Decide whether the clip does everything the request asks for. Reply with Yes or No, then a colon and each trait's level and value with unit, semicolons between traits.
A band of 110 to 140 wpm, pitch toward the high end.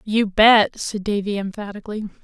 Yes: slow, 135 wpm; high, 205 Hz